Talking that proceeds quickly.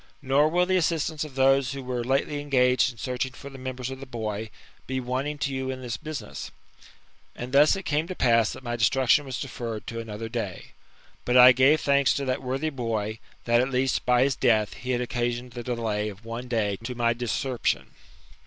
Yes: fast, 210 wpm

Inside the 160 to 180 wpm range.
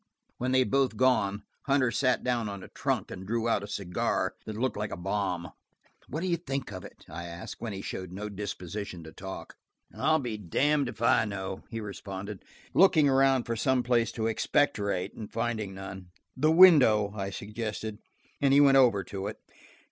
No: average, 195 wpm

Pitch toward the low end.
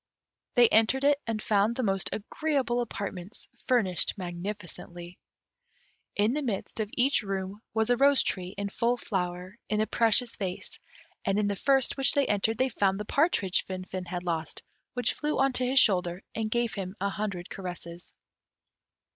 No: high, 210 Hz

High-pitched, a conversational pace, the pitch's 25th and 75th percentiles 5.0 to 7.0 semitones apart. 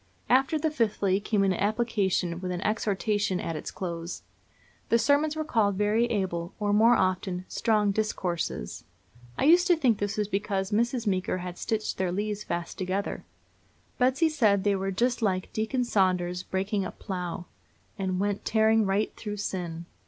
No: high, 205 Hz; average, 165 wpm; average, 3.2 semitones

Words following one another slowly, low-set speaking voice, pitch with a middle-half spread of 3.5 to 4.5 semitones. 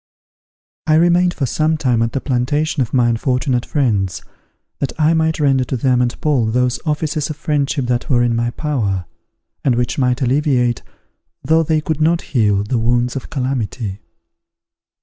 No: average, 170 wpm; low, 130 Hz; average, 4.0 semitones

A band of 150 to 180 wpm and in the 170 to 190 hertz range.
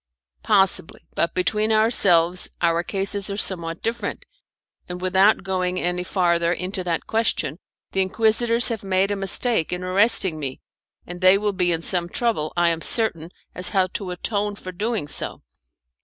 Yes: average, 165 wpm; medium, 185 Hz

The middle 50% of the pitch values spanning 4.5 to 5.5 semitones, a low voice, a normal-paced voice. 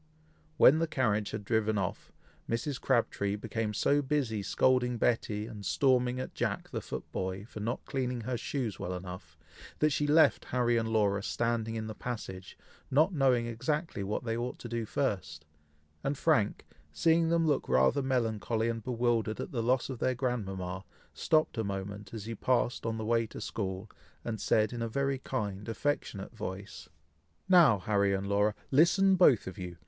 No: average, 4.0 semitones; low, 115 Hz; average, 175 wpm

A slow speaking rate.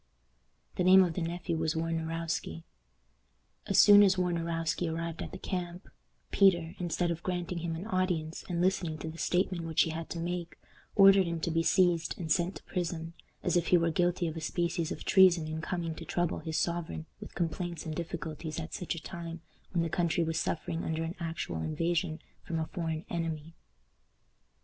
No: average, 190 wpm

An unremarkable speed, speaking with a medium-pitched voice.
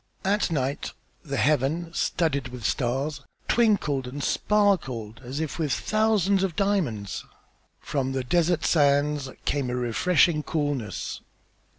No: slow, 120 wpm; medium, 145 Hz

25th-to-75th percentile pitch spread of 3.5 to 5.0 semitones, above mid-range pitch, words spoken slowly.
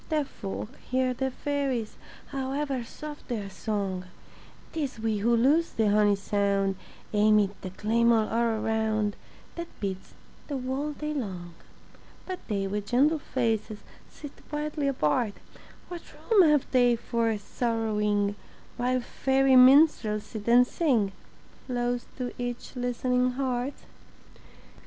Yes: average, 4.3 semitones; high, 240 Hz; slow, 125 wpm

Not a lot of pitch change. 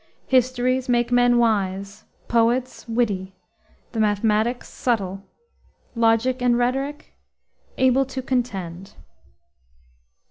No: average, 3.2 semitones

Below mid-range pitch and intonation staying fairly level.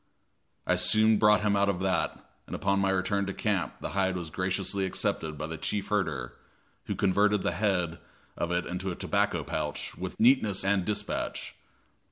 Yes: very low, 95 Hz; narrow, 2.1 semitones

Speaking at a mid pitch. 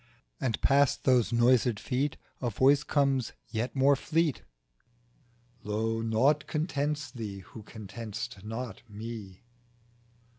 No: low, 120 Hz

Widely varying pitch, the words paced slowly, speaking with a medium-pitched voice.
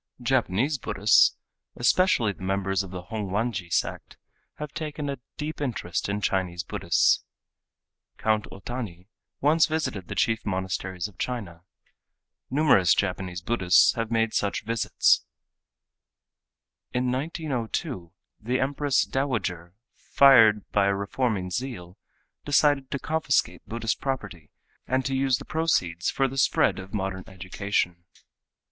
No: wide, 6.0 semitones; slow, 125 wpm; low, 110 Hz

